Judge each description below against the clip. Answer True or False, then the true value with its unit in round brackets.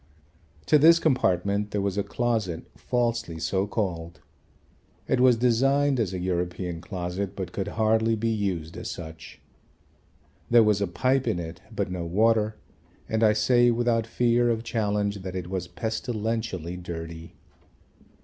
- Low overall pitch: True (105 Hz)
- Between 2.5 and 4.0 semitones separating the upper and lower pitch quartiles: False (4.4 semitones)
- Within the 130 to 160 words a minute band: True (150 wpm)